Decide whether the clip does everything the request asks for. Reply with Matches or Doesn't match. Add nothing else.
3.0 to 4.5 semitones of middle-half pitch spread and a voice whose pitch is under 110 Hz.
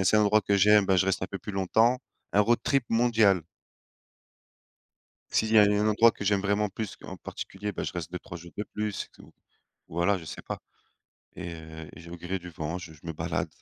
Matches